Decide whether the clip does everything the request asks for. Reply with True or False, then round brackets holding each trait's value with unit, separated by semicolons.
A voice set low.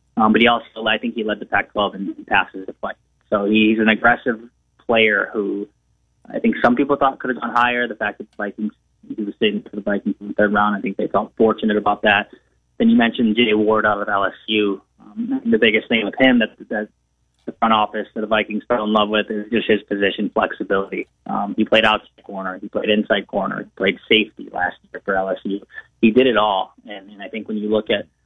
True (110 Hz)